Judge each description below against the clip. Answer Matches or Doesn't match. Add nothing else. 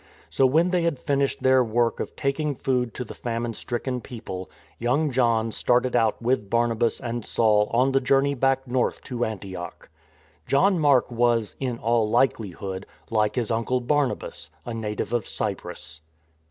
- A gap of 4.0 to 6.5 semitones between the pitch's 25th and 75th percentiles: Doesn't match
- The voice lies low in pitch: Matches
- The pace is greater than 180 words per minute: Doesn't match